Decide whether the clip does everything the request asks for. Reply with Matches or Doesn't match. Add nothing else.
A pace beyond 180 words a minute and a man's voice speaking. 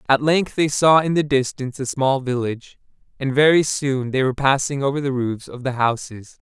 Matches